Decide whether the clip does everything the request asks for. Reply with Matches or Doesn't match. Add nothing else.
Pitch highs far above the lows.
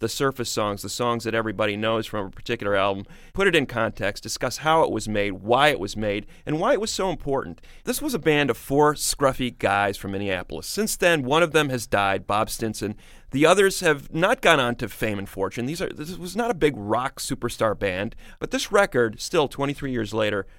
Matches